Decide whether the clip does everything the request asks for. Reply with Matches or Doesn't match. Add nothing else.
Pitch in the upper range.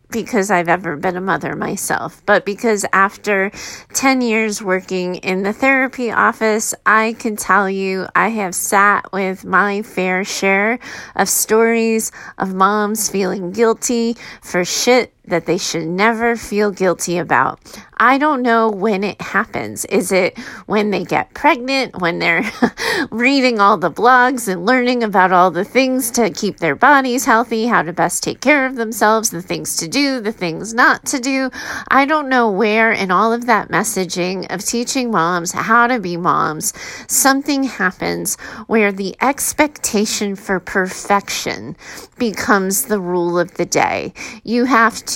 Matches